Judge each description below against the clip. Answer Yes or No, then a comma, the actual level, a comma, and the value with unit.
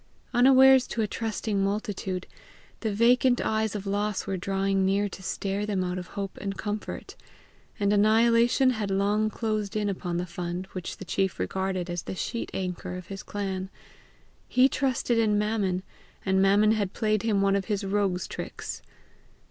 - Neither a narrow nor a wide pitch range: No, narrow, 2.3 semitones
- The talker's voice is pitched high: Yes, high, 200 Hz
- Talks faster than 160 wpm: Yes, average, 170 wpm